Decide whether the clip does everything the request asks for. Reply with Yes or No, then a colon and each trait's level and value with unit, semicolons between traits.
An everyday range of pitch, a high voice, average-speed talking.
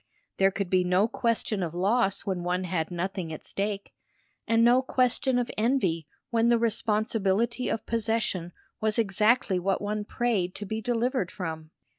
Yes: average, 4.0 semitones; high, 210 Hz; average, 160 wpm